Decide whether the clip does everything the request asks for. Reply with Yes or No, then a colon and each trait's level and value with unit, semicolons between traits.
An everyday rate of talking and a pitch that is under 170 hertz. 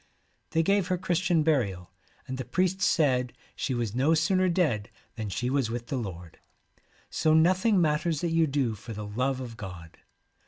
Yes: average, 180 wpm; low, 135 Hz